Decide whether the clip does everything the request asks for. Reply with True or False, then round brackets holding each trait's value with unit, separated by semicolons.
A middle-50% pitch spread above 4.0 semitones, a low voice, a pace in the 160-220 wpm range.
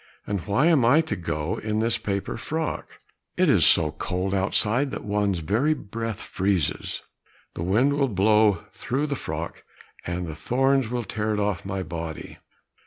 True (5.1 semitones; 105 Hz; 170 wpm)